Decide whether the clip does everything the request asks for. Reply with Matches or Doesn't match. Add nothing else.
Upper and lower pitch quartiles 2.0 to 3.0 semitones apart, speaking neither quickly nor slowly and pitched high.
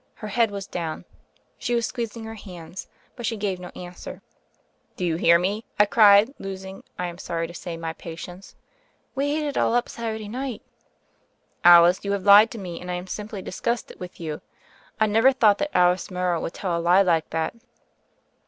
Doesn't match